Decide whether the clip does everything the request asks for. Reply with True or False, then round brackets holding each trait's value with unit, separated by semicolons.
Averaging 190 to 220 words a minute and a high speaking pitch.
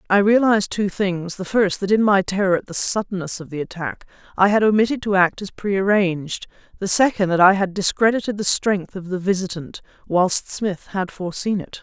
True (205 wpm; 195 Hz)